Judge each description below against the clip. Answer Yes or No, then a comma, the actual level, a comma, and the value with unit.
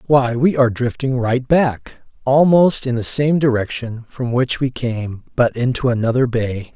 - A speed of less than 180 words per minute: Yes, average, 170 wpm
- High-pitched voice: No, low, 125 Hz